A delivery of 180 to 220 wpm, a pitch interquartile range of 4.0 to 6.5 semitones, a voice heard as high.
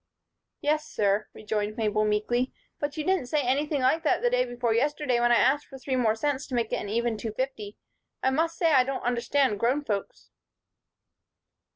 Yes: average, 190 wpm; average, 4.4 semitones; very high, 250 Hz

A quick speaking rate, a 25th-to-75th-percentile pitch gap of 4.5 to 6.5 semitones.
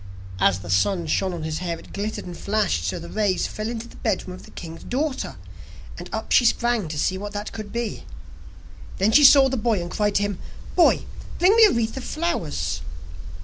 Yes: fast, 220 wpm; wide, 5.5 semitones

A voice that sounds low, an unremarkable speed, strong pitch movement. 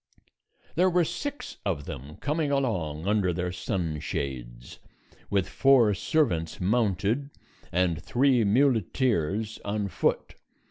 No: low, 100 Hz; slow, 110 wpm; wide, 7.4 semitones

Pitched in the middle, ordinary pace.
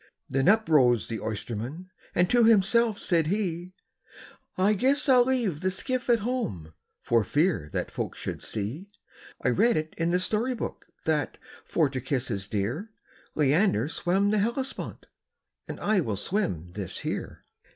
Yes: medium, 175 Hz; average, 160 wpm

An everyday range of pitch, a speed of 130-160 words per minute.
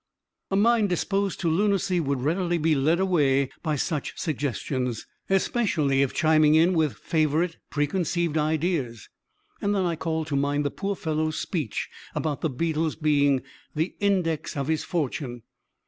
Yes: average, 3.6 semitones; average, 150 wpm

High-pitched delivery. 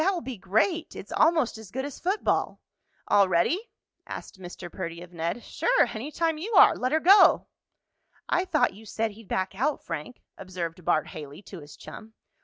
Yes: high, 220 Hz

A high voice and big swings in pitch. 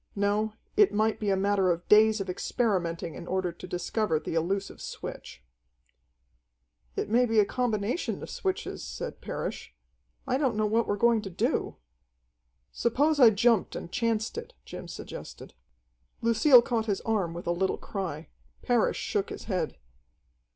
No: high, 210 Hz; average, 3.8 semitones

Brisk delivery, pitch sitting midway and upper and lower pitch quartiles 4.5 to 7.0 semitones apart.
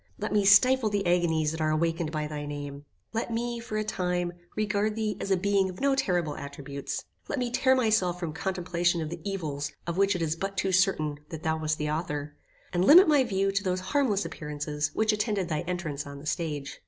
Yes: fast, 215 wpm; medium, 180 Hz; average, 5.0 semitones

